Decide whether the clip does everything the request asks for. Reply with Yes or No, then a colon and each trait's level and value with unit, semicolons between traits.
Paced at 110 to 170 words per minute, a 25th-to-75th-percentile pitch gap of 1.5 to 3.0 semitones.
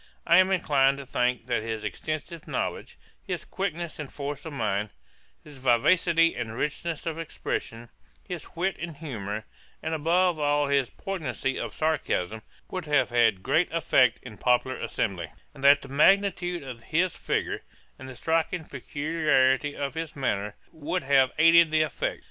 No: average, 160 wpm; average, 4.7 semitones